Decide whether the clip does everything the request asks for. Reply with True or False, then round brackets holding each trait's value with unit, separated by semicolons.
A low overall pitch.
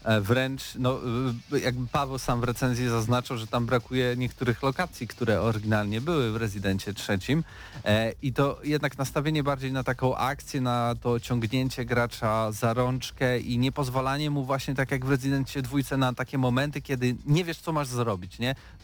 True (125 Hz)